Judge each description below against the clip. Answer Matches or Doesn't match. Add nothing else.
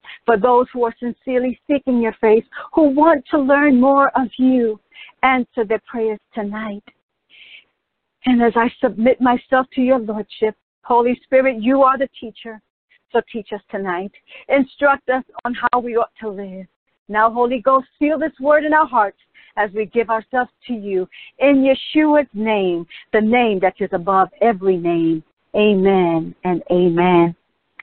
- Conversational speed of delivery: Matches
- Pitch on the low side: Doesn't match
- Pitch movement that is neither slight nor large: Matches